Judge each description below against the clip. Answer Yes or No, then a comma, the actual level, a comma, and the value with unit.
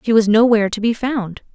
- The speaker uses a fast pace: Yes, fast, 235 wpm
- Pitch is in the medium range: No, high, 220 Hz